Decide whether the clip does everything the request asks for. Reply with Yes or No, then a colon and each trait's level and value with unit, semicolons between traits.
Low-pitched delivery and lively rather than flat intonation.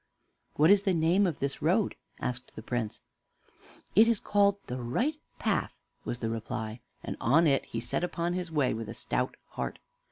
No: medium, 150 Hz; wide, 7.4 semitones